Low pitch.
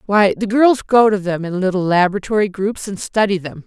No: high, 200 Hz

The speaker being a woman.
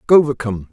No: male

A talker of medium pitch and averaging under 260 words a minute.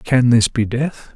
No: low, 120 Hz; fast, 205 wpm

